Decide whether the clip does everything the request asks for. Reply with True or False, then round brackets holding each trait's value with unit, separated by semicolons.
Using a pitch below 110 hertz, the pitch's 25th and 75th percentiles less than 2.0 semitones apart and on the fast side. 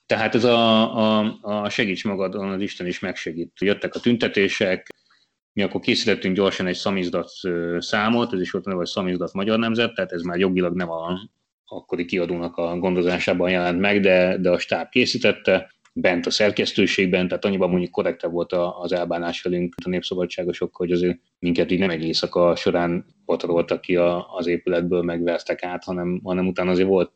True (90 Hz; 1.6 semitones; 170 wpm)